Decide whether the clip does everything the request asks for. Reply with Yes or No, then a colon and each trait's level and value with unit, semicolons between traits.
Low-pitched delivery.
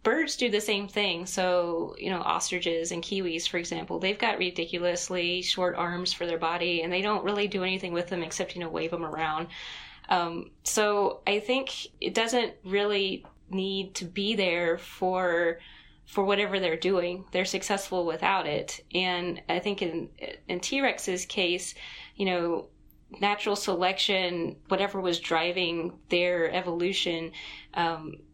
No: medium, 180 Hz